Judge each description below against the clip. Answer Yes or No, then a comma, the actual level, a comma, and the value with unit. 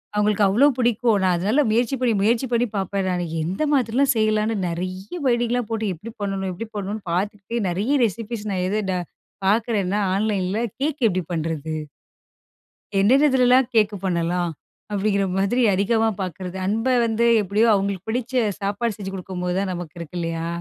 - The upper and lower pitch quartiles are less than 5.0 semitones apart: Yes, average, 3.7 semitones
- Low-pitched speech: No, high, 205 Hz